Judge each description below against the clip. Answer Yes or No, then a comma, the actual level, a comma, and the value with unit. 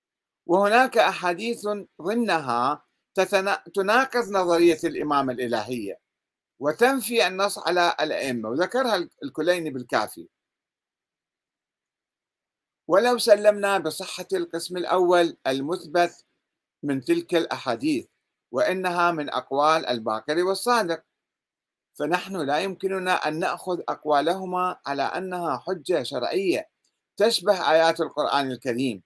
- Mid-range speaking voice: Yes, medium, 180 Hz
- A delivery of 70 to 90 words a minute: Yes, average, 85 wpm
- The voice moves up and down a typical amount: Yes, average, 4.6 semitones